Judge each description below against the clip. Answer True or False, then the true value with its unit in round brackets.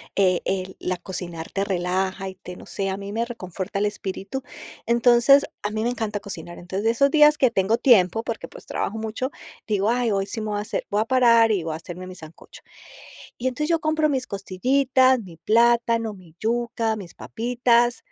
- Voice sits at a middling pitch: False (215 Hz)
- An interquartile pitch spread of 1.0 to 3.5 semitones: False (4.1 semitones)